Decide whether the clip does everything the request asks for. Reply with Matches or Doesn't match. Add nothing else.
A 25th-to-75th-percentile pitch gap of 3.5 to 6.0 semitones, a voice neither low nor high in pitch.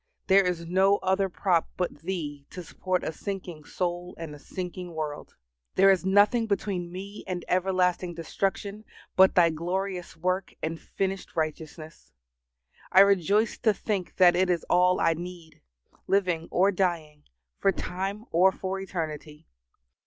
Doesn't match